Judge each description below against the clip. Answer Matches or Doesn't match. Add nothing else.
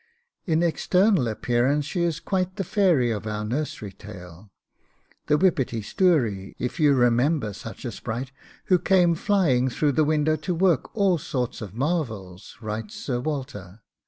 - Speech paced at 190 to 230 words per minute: Doesn't match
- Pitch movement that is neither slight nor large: Doesn't match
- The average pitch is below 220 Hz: Matches